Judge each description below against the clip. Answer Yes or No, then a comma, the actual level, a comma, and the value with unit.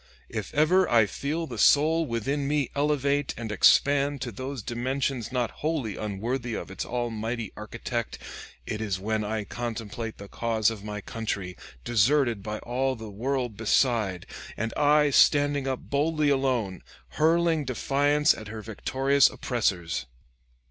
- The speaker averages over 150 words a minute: No, average, 140 wpm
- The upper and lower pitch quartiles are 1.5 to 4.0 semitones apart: No, average, 4.5 semitones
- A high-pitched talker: No, low, 120 Hz